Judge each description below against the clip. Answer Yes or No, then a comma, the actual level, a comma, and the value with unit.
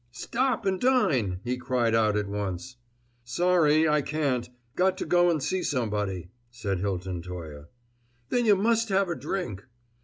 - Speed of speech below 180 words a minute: Yes, average, 155 wpm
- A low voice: Yes, low, 125 Hz